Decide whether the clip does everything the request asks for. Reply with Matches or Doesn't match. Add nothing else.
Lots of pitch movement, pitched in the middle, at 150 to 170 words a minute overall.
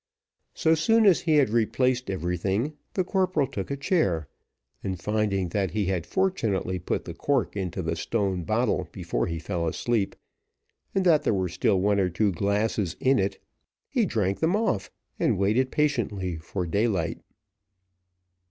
Doesn't match